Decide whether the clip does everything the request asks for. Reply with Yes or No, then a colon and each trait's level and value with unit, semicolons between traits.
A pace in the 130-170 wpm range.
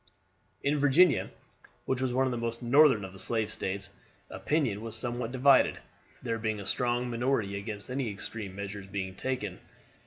Yes: average, 165 wpm